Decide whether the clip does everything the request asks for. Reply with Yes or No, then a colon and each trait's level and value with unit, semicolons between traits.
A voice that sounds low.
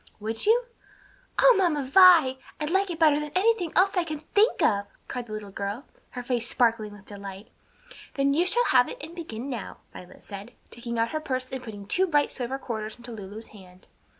No: very high, 255 Hz